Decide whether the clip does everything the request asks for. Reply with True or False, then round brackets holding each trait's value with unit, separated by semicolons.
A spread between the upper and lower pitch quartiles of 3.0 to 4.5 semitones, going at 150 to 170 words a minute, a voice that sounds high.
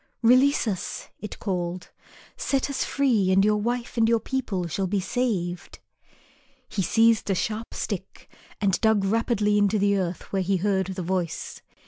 True (3.4 semitones; 165 wpm; 205 Hz)